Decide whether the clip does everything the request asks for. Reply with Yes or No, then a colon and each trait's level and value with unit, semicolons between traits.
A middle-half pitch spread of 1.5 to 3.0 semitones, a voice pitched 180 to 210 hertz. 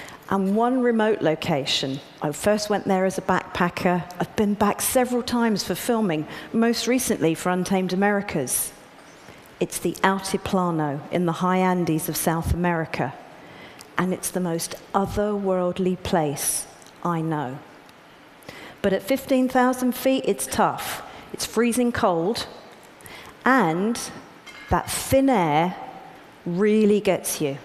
No: average, 4.3 semitones; high, 190 Hz